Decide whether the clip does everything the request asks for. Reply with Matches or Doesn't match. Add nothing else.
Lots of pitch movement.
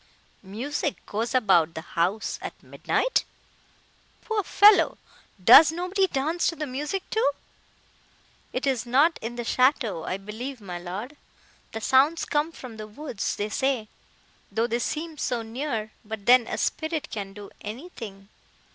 Matches